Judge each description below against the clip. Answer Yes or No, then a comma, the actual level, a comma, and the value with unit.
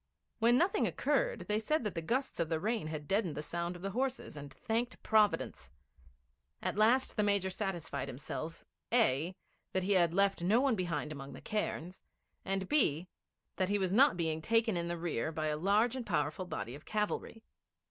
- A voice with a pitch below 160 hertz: No, high, 190 Hz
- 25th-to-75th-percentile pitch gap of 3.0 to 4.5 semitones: No, wide, 5.4 semitones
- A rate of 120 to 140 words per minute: No, average, 190 wpm